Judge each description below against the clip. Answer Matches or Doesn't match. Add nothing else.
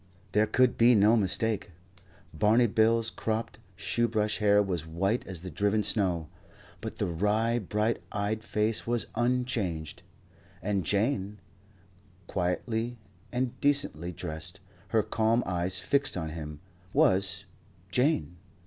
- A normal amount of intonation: Matches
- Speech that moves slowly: Matches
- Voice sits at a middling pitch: Doesn't match